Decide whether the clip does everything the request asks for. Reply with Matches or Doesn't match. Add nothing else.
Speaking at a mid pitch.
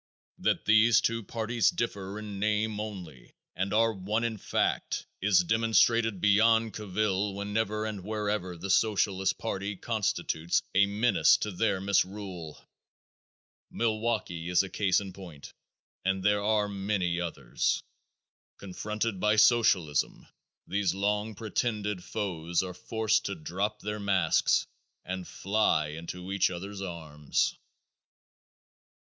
Doesn't match